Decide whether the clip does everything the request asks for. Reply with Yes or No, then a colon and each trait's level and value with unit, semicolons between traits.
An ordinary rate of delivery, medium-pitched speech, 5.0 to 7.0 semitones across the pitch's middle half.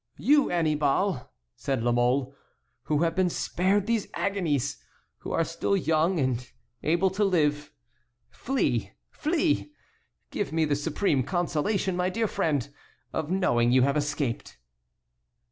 No: slow, 130 wpm; medium, 160 Hz; average, 5.3 semitones